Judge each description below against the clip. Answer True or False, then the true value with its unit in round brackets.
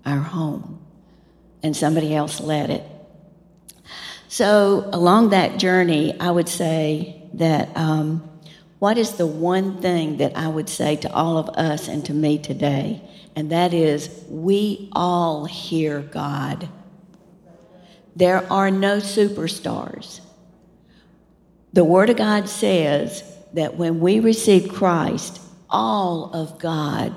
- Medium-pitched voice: True (175 Hz)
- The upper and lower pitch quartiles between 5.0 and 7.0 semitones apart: False (3.3 semitones)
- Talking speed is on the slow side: True (125 wpm)